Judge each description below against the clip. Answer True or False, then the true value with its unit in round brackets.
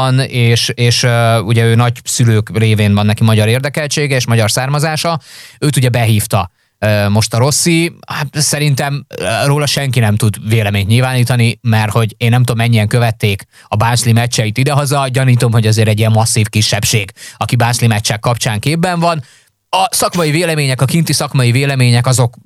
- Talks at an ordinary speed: False (165 wpm)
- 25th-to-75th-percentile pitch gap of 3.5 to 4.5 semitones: True (4.0 semitones)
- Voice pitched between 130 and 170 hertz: False (120 Hz)